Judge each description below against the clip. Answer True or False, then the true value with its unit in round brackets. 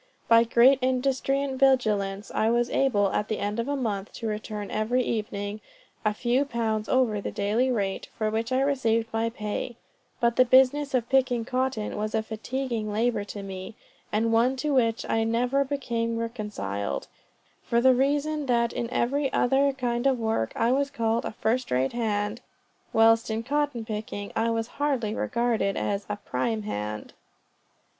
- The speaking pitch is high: True (230 Hz)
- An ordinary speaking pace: True (170 wpm)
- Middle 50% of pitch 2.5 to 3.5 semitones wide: True (3.2 semitones)